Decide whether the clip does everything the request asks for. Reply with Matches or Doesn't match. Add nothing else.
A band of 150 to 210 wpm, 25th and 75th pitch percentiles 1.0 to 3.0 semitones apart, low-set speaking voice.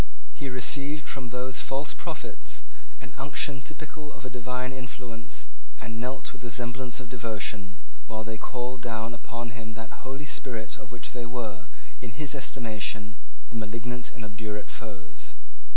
Matches